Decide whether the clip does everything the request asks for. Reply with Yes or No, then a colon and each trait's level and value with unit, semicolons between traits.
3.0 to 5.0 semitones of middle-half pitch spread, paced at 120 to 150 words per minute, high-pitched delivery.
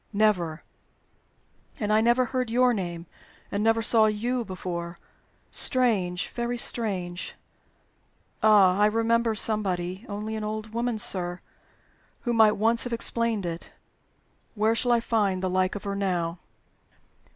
Yes: average, 3.7 semitones; slow, 135 wpm; high, 215 Hz